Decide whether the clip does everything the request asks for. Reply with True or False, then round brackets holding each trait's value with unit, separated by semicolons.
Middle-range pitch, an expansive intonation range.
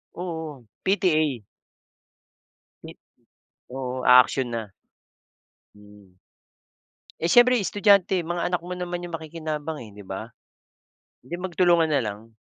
True (160 Hz; 6.0 semitones)